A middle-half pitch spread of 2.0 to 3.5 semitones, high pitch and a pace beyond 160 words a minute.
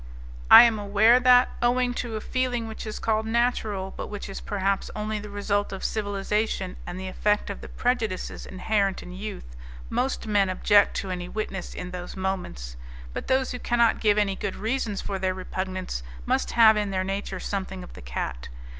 Yes: average, 2.8 semitones; high, 205 Hz; average, 190 wpm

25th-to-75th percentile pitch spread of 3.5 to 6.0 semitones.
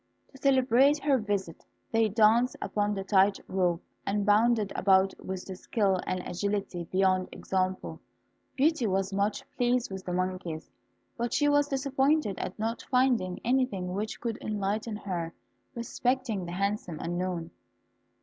Yes: average, 4.5 semitones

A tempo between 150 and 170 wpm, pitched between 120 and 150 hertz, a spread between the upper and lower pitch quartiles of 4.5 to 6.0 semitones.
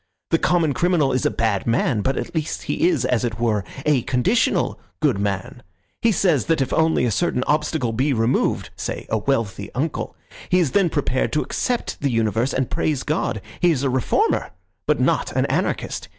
No: average, 190 wpm; low, 135 Hz; wide, 5.5 semitones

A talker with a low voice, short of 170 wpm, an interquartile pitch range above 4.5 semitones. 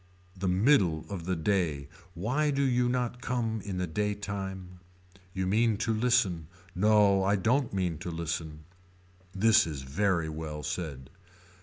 Yes: very low, 95 Hz; average, 150 wpm; average, 5.0 semitones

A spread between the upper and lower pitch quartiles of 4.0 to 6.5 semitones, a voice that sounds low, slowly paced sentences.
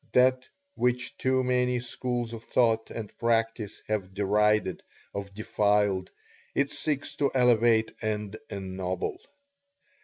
No: average, 3.3 semitones; low, 115 Hz; slow, 115 wpm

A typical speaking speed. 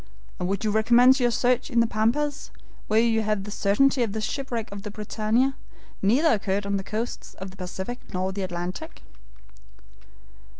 Yes: average, 175 wpm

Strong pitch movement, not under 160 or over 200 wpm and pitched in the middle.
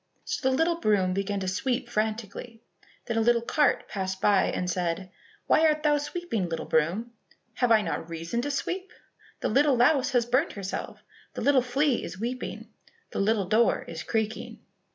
No: wide, 5.7 semitones; average, 175 wpm; high, 230 Hz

